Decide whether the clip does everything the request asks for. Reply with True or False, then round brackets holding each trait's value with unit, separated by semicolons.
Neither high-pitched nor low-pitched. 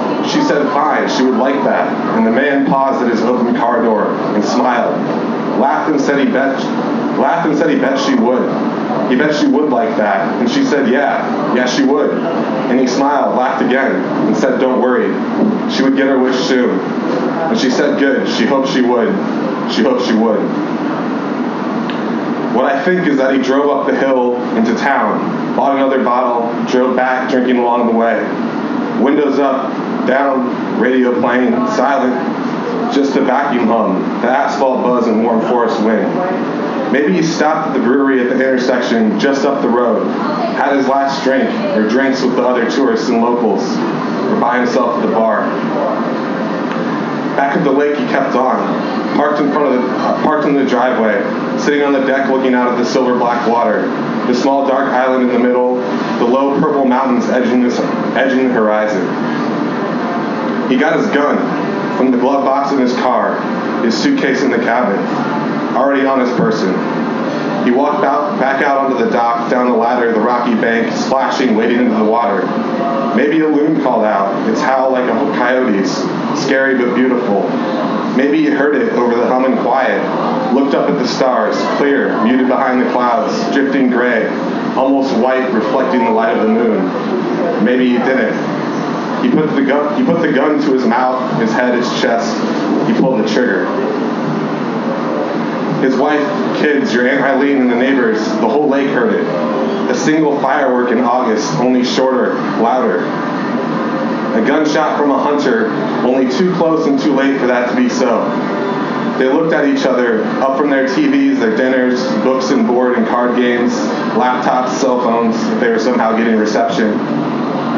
False (130 Hz)